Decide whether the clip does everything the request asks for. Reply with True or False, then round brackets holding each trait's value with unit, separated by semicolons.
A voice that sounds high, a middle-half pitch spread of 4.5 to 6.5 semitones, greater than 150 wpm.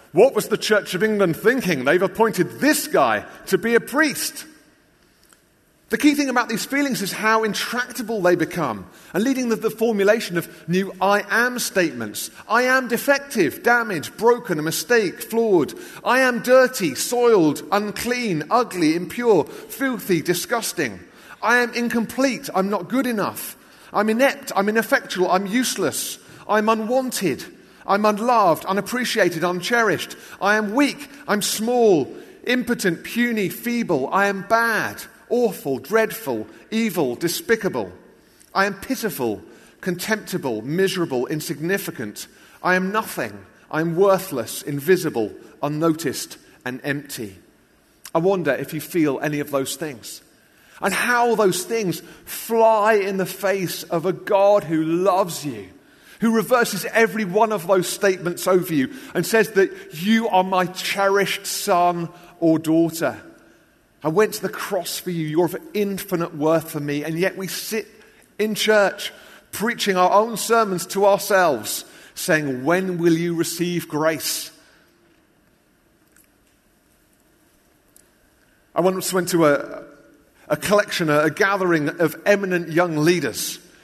False (195 Hz; 5.1 semitones; 135 wpm)